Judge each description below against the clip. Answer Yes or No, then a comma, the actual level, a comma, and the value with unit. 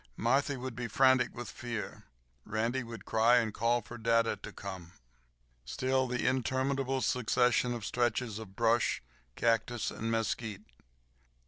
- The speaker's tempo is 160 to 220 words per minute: No, slow, 135 wpm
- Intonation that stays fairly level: Yes, narrow, 2.0 semitones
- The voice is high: No, low, 120 Hz